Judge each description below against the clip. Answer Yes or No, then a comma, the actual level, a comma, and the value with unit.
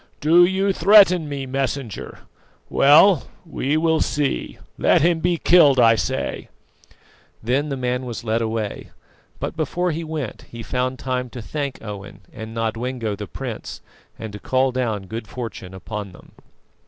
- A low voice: Yes, low, 130 Hz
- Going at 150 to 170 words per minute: Yes, average, 155 wpm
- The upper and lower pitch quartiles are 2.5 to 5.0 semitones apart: No, wide, 5.6 semitones